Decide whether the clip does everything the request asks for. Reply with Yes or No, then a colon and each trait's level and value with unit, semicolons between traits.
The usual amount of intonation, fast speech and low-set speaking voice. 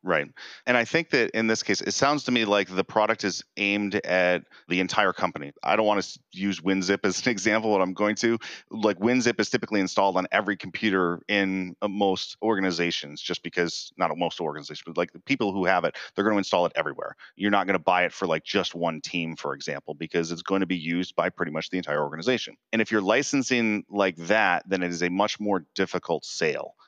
Yes: average, 3.1 semitones; fast, 230 wpm; low, 100 Hz